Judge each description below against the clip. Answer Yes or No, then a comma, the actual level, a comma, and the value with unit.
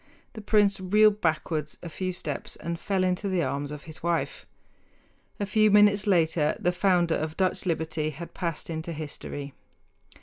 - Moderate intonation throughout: Yes, average, 3.8 semitones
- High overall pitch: No, medium, 170 Hz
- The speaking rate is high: No, average, 165 wpm